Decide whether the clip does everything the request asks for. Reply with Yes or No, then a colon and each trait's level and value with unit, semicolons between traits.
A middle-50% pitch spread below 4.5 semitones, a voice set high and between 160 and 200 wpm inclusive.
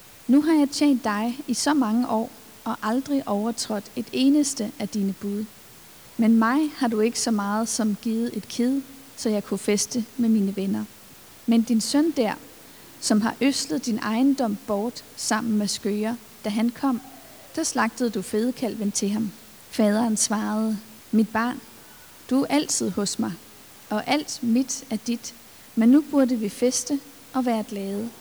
Yes: average, 3.3 semitones; high, 230 Hz; average, 170 wpm